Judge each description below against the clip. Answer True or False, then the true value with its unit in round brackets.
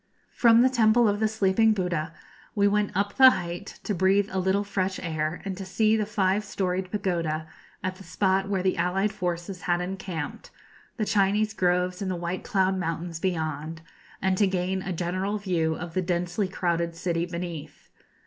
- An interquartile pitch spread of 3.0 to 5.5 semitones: False (2.6 semitones)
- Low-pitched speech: False (185 Hz)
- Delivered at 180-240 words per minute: True (185 wpm)